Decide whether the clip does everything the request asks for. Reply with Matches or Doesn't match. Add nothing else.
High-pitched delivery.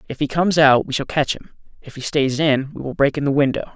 Doesn't match